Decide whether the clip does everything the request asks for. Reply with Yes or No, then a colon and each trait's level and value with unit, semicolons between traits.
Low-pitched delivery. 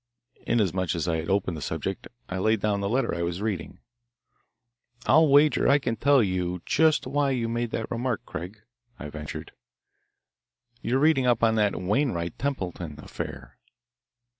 Yes: low, 105 Hz